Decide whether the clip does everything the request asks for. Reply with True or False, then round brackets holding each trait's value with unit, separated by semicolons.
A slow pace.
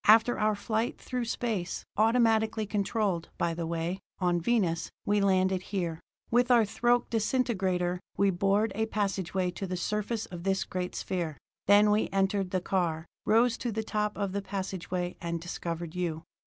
False (165 wpm)